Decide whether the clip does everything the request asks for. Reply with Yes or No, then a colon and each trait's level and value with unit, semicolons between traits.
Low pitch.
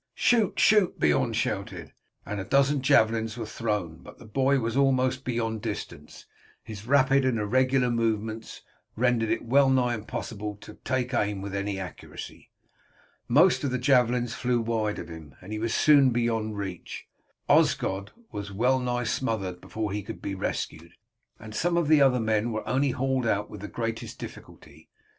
Yes: low, 115 Hz